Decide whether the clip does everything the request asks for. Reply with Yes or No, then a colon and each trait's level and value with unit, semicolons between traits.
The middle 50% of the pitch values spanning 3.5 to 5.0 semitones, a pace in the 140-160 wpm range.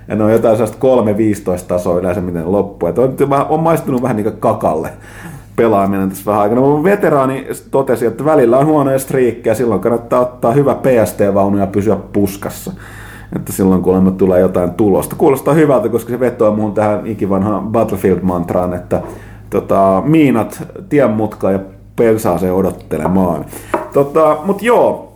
Yes: average, 4.7 semitones; fast, 155 wpm